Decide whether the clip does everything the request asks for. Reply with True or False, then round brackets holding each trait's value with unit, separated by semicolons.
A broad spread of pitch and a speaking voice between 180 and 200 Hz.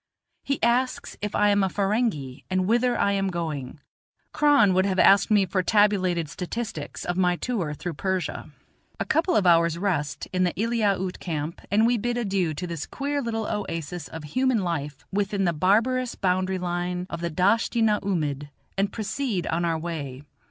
False (4.3 semitones; 190 Hz)